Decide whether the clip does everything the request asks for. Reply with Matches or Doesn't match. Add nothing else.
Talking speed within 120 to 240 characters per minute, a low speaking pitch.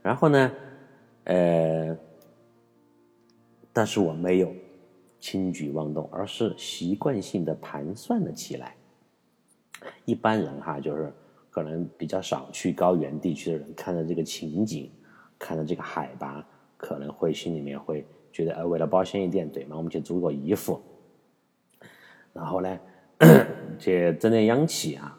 Matches